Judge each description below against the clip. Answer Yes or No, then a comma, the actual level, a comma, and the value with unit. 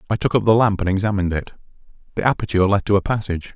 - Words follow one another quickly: Yes, fast, 235 wpm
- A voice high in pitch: No, low, 100 Hz